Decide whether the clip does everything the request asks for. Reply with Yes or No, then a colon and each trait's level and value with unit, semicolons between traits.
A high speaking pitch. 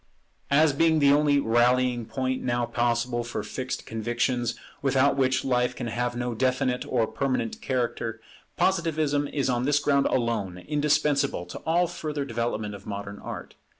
No: low, 130 Hz